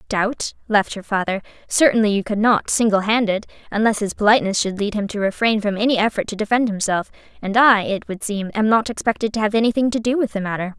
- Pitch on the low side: No, high, 215 Hz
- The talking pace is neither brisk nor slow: No, fast, 220 wpm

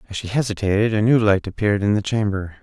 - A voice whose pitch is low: Yes, low, 105 Hz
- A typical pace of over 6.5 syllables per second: Yes, 6.7 syllables/s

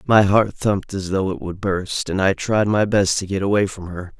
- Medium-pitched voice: No, very low, 95 Hz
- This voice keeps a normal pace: No, fast, 260 wpm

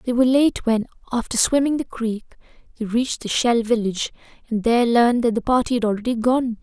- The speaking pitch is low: No, high, 235 Hz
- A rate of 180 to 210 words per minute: Yes, average, 200 wpm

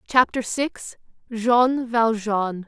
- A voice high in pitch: Yes, high, 230 Hz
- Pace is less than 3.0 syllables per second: Yes, 2.8 syllables/s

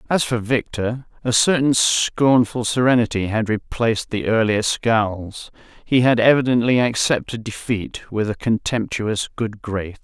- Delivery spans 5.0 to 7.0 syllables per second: No, 4.3 syllables/s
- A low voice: Yes, low, 115 Hz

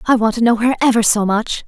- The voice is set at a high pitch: Yes, high, 225 Hz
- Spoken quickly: Yes, fast, 285 wpm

